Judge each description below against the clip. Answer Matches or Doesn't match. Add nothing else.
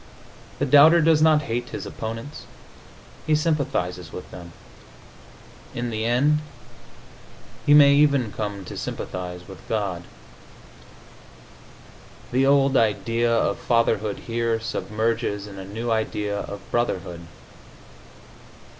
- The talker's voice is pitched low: Matches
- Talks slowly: Matches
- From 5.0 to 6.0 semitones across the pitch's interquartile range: Matches